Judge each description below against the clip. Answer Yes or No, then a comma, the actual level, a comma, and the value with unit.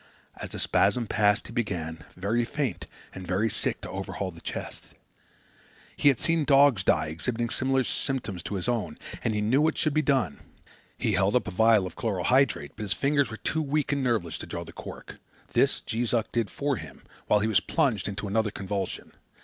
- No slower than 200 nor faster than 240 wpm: Yes, fast, 205 wpm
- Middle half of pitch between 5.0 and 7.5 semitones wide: Yes, wide, 5.4 semitones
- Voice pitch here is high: No, low, 110 Hz